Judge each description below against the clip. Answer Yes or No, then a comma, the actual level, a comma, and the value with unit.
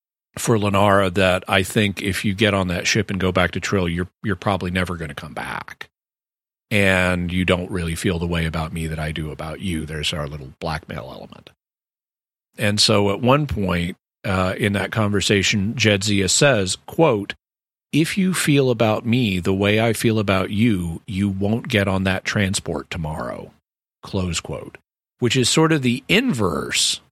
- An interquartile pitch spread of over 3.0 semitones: Yes, average, 3.4 semitones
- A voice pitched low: Yes, low, 100 Hz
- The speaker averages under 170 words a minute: No, average, 180 wpm